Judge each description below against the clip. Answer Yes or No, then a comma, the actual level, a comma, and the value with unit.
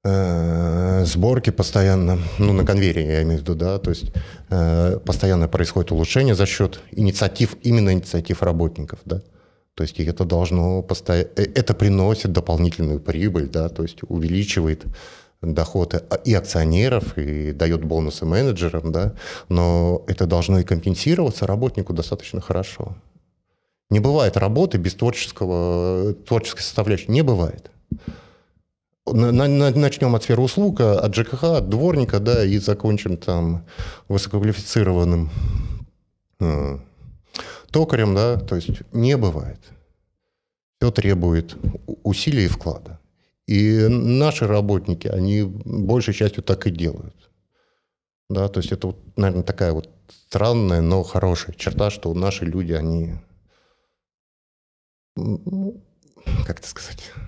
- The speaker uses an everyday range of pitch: Yes, average, 3.9 semitones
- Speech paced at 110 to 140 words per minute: Yes, average, 115 wpm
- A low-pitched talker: Yes, very low, 95 Hz